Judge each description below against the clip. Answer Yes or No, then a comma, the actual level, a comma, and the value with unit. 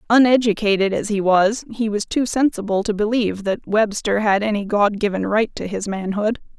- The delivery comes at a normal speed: Yes, average, 180 wpm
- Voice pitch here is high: Yes, high, 210 Hz